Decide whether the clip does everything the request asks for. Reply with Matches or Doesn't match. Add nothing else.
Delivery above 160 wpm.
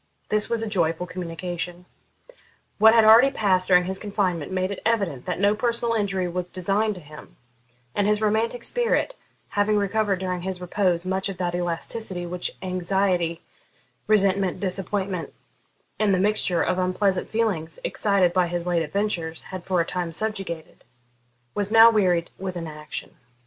Doesn't match